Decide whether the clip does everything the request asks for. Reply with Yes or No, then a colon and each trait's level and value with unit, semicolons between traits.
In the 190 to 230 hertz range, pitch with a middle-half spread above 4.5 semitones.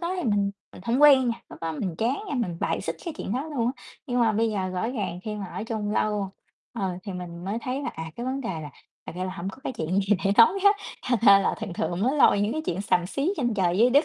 Yes: high, 215 Hz; average, 5.0 semitones